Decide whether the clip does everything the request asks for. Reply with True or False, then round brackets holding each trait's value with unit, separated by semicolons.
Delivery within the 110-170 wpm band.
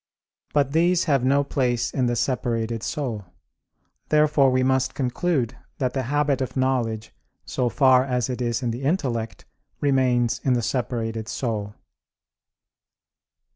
True (135 wpm)